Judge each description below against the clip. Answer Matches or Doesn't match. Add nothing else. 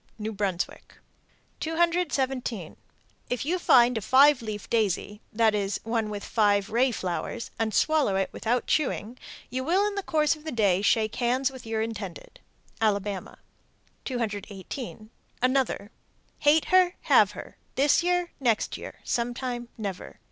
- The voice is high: Matches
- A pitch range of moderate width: Matches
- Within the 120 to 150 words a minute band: Matches